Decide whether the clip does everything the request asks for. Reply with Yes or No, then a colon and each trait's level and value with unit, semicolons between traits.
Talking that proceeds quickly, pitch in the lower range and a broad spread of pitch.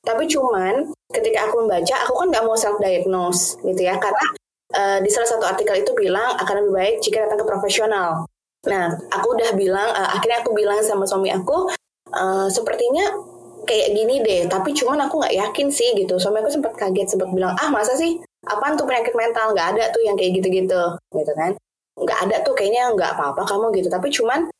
No: fast, 200 wpm; high, 220 Hz; wide, 8.1 semitones